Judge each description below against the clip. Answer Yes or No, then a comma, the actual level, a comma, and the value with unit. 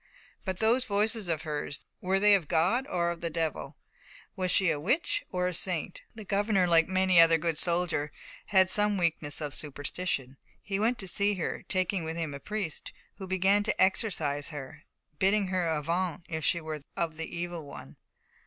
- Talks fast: No, average, 180 wpm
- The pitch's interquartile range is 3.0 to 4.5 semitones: Yes, average, 3.5 semitones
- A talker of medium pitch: Yes, medium, 175 Hz